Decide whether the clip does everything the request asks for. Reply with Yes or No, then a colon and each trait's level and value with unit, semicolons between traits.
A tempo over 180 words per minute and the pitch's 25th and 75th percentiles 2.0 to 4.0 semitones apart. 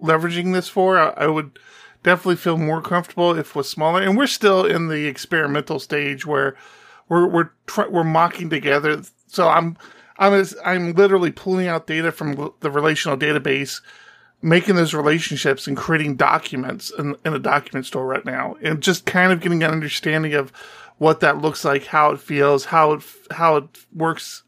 No: average, 175 wpm; average, 2.9 semitones